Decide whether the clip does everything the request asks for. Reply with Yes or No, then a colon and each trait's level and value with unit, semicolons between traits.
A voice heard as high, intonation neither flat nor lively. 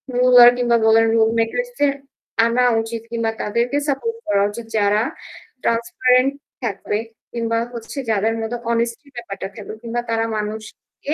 No: high, 230 Hz; narrow, 1.9 semitones